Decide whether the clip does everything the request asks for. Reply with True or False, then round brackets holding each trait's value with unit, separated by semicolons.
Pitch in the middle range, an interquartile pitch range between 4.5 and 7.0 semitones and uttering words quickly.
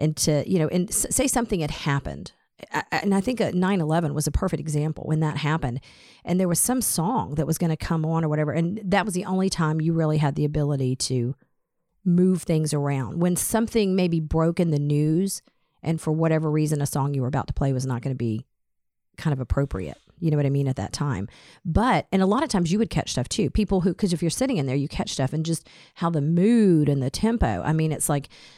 False (160 Hz; 4.0 semitones; 250 wpm)